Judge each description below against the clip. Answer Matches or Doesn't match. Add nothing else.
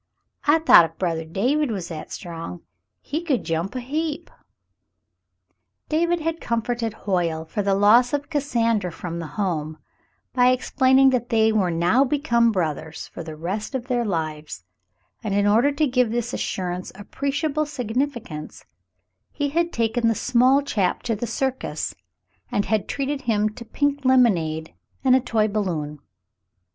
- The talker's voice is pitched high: Matches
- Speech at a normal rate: Matches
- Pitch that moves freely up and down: Matches